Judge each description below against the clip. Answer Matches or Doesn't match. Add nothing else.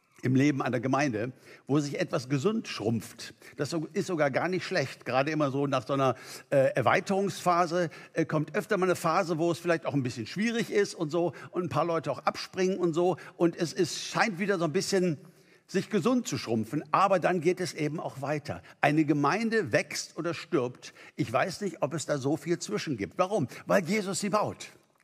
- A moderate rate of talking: Doesn't match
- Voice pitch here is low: Doesn't match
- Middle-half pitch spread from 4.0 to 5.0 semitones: Matches